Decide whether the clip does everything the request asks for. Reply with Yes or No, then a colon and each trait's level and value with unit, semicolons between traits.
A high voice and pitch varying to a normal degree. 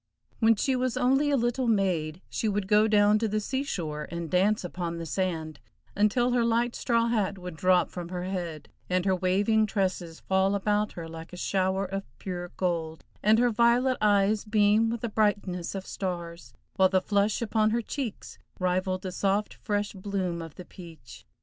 Yes: high, 195 Hz; average, 3.3 semitones